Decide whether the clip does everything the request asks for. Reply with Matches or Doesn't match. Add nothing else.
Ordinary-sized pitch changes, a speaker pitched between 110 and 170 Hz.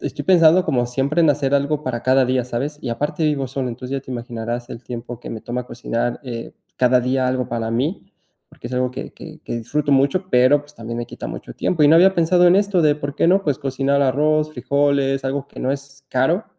Matches